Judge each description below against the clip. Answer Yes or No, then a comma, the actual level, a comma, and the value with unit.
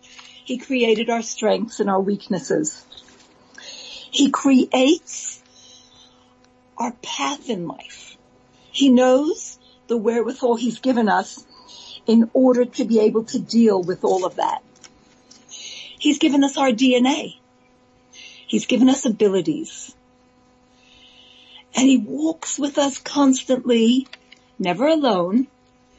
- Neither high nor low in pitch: No, very high, 250 Hz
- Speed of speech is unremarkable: No, slow, 110 wpm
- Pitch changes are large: No, average, 3.4 semitones